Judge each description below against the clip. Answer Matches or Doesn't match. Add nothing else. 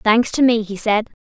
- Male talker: Doesn't match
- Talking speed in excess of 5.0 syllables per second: Doesn't match